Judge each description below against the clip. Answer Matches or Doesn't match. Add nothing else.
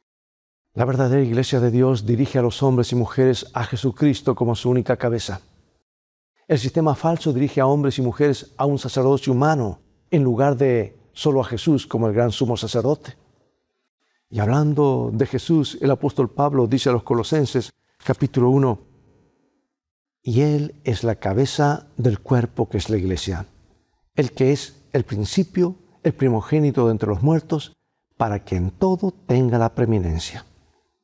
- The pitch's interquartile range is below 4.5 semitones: Matches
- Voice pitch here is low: Matches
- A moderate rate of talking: Matches